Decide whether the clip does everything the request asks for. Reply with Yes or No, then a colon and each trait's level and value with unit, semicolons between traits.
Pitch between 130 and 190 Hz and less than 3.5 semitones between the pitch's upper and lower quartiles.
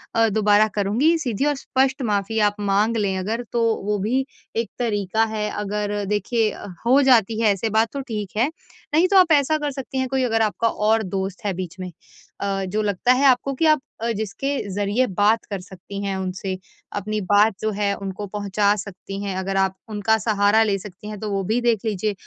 No: high, 210 Hz; average, 2.8 semitones